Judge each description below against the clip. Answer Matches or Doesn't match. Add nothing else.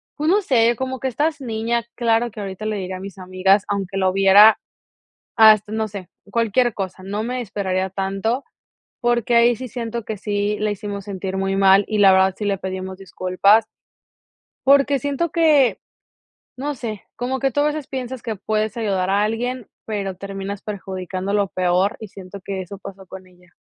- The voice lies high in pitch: Matches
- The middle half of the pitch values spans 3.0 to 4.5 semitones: Matches